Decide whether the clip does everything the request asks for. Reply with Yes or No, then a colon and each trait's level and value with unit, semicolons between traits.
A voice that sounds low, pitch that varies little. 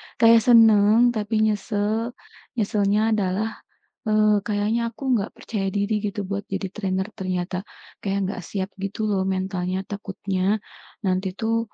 No: high, 205 Hz; narrow, 2.1 semitones